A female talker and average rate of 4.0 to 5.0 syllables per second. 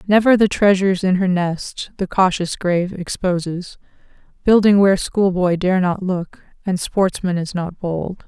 Yes: female; 4.4 syllables/s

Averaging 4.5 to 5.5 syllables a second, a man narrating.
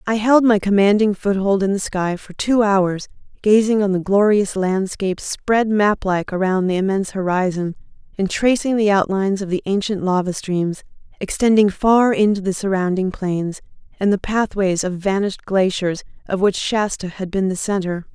No: 5.0 syllables/s; female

